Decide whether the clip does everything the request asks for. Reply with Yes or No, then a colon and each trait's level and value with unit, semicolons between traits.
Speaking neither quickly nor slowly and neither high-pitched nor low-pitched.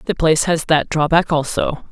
Yes: average, 190 wpm; medium, 160 Hz